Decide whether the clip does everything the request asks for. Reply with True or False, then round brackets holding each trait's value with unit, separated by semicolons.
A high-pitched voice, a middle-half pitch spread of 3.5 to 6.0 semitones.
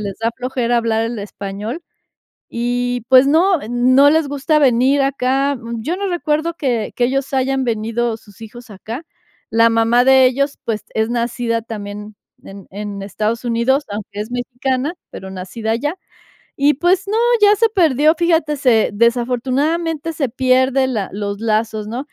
True (245 Hz; 3.9 semitones)